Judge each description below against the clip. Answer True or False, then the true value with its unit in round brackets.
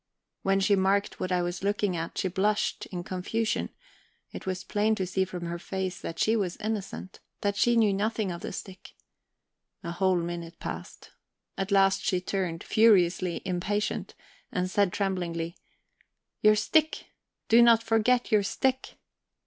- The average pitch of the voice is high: True (195 Hz)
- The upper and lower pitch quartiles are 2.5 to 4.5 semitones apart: True (2.8 semitones)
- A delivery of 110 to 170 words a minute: True (155 wpm)